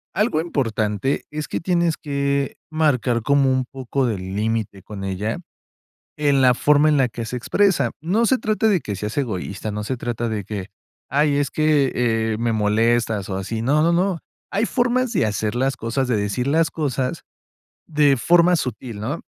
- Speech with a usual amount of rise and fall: No, wide, 5.7 semitones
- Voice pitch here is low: Yes, low, 130 Hz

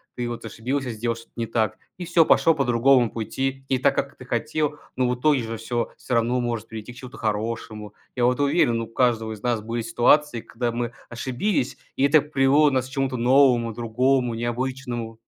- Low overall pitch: Yes, low, 120 Hz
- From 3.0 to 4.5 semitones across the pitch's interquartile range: No, narrow, 2.6 semitones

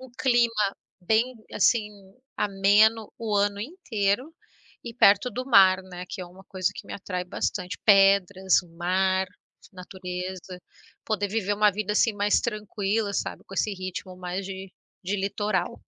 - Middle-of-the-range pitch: No, high, 200 Hz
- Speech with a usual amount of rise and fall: No, narrow, 2.3 semitones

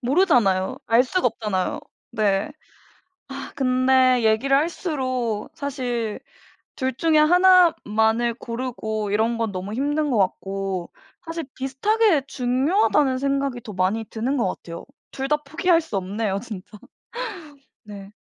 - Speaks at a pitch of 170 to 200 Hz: No, high, 245 Hz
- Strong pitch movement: No, average, 4.8 semitones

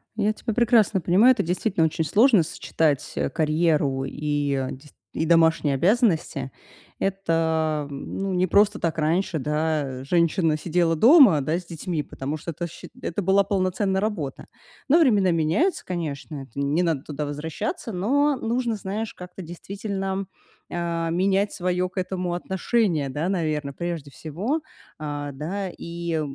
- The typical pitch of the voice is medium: Yes, medium, 170 Hz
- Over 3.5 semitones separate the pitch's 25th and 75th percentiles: Yes, average, 4.3 semitones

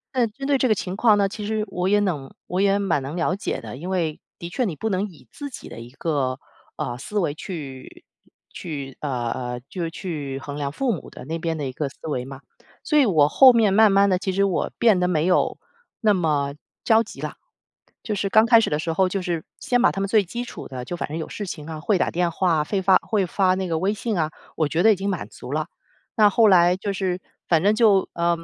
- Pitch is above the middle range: No, medium, 180 Hz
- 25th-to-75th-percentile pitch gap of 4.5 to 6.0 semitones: Yes, average, 5.0 semitones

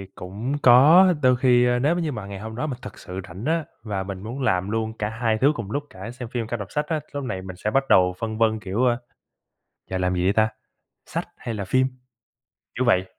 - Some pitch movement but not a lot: Yes, average, 4.6 semitones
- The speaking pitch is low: Yes, low, 115 Hz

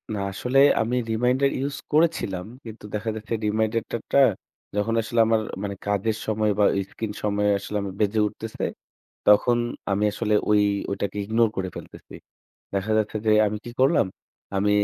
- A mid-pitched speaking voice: No, low, 110 Hz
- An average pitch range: No, narrow, 2.0 semitones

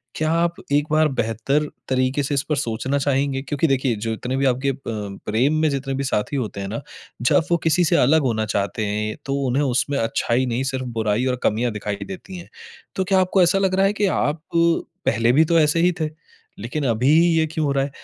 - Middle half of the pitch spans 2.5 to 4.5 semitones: No, average, 5.0 semitones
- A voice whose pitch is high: No, low, 135 Hz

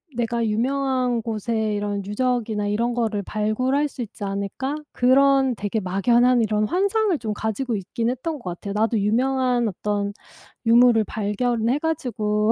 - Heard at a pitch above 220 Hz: Yes, high, 230 Hz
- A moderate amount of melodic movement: Yes, average, 3.4 semitones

